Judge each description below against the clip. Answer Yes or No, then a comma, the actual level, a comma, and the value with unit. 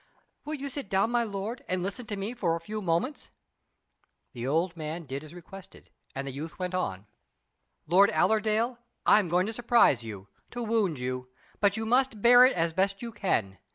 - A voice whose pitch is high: Yes, high, 195 Hz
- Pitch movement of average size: No, wide, 5.7 semitones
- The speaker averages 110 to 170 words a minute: No, average, 195 wpm